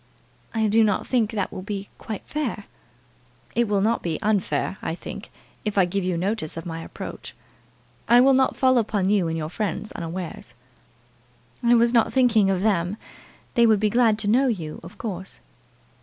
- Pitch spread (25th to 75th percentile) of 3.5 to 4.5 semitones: Yes, average, 3.9 semitones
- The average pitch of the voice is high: Yes, high, 210 Hz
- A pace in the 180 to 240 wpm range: Yes, average, 185 wpm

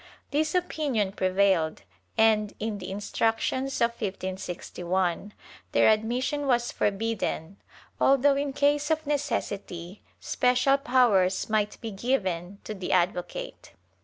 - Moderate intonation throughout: No, wide, 5.9 semitones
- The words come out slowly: Yes, slow, 110 wpm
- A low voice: No, high, 220 Hz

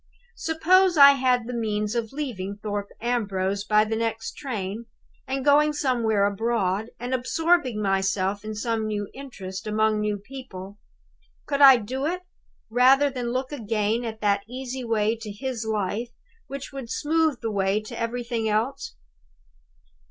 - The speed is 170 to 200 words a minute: No, average, 150 wpm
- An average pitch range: Yes, average, 4.0 semitones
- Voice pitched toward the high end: Yes, high, 230 Hz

